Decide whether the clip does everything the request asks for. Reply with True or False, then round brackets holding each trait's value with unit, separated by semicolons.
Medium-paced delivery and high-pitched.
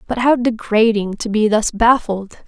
True (170 wpm; 220 Hz)